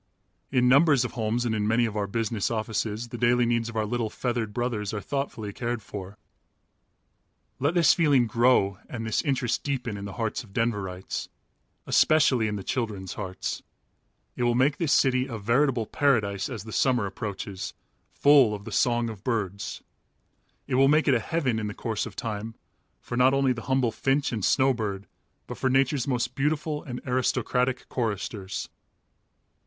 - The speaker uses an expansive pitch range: No, average, 3.7 semitones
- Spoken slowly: No, average, 175 wpm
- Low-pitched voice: Yes, low, 120 Hz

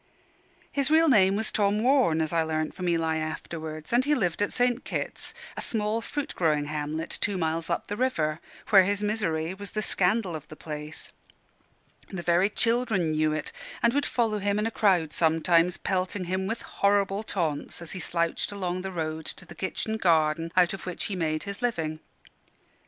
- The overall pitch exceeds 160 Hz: Yes, medium, 185 Hz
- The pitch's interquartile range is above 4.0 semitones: Yes, average, 4.7 semitones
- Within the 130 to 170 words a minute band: No, average, 190 wpm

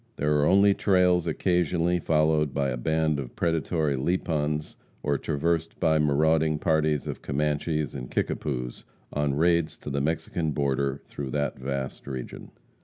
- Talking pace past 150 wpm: No, average, 145 wpm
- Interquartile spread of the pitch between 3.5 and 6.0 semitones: No, narrow, 2.5 semitones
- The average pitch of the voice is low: Yes, very low, 75 Hz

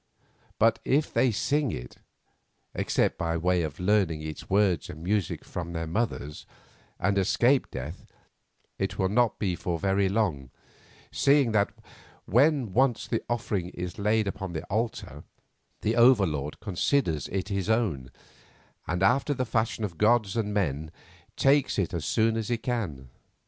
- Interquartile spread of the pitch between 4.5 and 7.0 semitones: Yes, average, 5.2 semitones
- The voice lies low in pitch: Yes, low, 100 Hz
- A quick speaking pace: No, average, 155 wpm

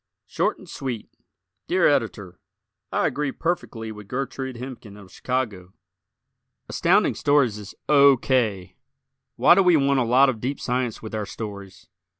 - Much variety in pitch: No, average, 4.6 semitones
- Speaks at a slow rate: No, average, 150 wpm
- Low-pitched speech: Yes, low, 125 Hz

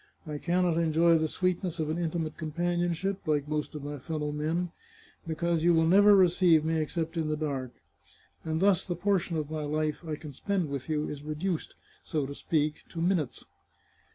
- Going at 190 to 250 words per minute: Yes, average, 195 wpm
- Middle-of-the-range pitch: Yes, medium, 160 Hz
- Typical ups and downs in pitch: No, narrow, 2.3 semitones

